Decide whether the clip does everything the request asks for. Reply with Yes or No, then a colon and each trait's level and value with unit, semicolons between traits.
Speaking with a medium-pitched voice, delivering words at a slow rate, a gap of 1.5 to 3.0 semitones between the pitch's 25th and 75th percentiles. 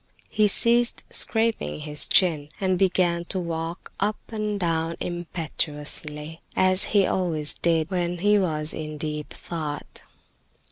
No: medium, 170 Hz; slow, 130 wpm; average, 3.7 semitones